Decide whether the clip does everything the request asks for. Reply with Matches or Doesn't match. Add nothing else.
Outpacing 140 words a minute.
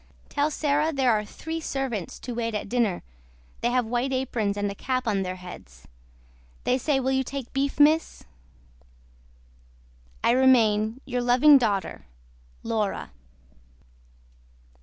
Doesn't match